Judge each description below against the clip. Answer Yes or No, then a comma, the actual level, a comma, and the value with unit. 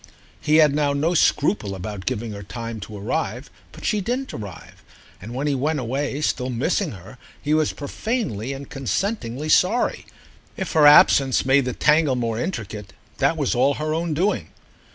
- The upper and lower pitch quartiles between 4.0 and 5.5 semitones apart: Yes, average, 5.1 semitones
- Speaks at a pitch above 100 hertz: Yes, medium, 140 Hz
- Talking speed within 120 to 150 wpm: No, average, 175 wpm